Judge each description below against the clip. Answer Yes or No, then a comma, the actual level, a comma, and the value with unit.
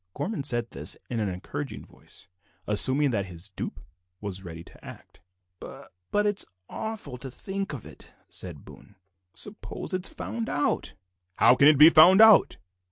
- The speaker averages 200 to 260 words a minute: No, average, 160 wpm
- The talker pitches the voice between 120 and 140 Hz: Yes, low, 135 Hz